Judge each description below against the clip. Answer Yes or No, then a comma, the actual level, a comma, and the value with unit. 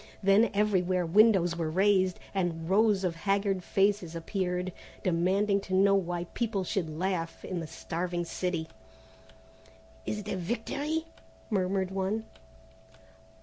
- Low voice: No, high, 190 Hz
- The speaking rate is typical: No, slow, 125 wpm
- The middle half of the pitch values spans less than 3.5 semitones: Yes, narrow, 2.5 semitones